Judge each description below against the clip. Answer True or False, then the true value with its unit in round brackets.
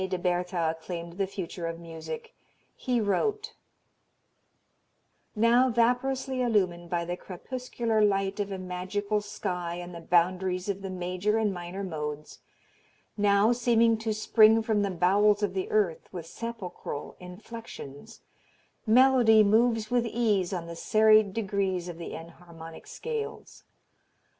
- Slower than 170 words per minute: True (135 wpm)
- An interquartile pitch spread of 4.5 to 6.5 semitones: False (4.0 semitones)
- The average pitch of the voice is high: True (200 Hz)